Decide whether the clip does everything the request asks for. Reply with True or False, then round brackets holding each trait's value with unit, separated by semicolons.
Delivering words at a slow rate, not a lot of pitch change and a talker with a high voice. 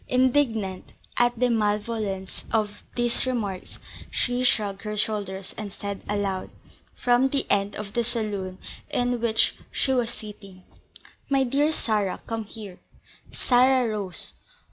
False (130 wpm; 3.4 semitones; 215 Hz)